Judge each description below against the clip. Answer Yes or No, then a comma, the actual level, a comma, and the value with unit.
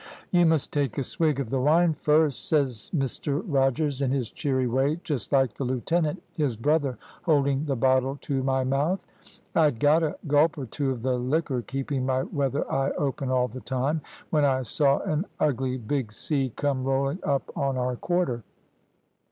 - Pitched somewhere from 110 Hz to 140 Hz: Yes, low, 135 Hz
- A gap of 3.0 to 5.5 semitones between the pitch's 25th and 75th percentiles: No, narrow, 2.5 semitones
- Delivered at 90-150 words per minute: No, average, 180 wpm